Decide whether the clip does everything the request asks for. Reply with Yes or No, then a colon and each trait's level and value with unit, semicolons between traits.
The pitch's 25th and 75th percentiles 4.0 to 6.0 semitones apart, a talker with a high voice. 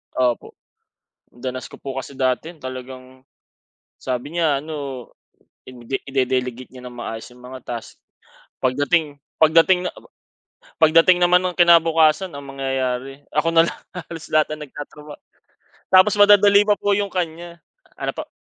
No: average, 4.8 semitones; medium, 145 Hz